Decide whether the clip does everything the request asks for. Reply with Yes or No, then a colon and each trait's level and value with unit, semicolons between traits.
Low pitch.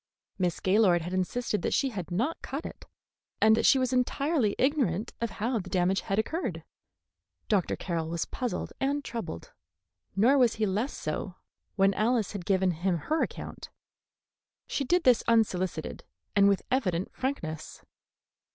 No: high, 210 Hz